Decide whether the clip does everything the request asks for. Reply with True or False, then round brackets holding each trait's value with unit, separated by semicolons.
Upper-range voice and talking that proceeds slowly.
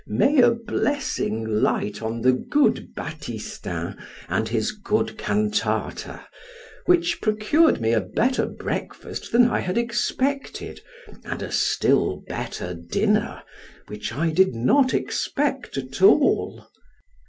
True (210 Hz; 120 wpm)